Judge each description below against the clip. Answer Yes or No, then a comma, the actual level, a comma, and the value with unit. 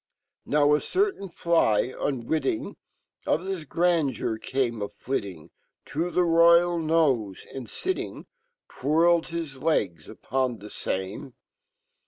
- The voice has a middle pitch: Yes, medium, 150 Hz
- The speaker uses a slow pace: Yes, slow, 115 wpm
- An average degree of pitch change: No, wide, 6.3 semitones